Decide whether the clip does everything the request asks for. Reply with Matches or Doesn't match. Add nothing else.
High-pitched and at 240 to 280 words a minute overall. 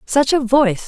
Doesn't match